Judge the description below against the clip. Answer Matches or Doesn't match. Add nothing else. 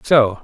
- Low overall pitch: Matches